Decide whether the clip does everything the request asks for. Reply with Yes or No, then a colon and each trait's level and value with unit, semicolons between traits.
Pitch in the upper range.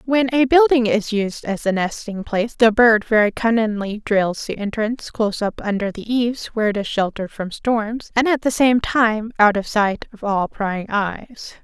Yes: high, 220 Hz